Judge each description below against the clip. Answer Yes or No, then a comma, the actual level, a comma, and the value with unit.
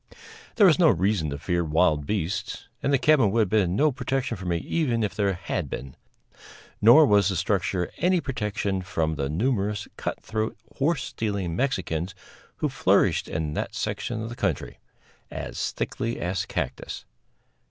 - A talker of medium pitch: No, low, 100 Hz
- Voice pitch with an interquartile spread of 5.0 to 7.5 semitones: Yes, wide, 5.4 semitones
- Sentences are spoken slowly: No, average, 165 wpm